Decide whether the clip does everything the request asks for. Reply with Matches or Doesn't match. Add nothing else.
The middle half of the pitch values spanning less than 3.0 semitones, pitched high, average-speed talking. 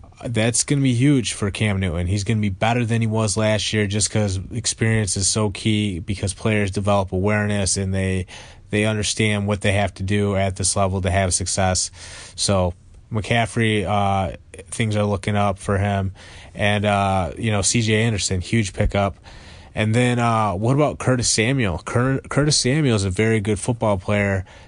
Doesn't match